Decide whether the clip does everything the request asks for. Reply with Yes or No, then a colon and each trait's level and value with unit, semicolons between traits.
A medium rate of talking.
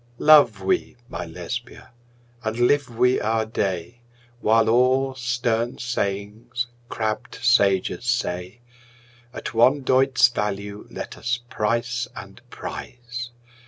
No: slow, 110 wpm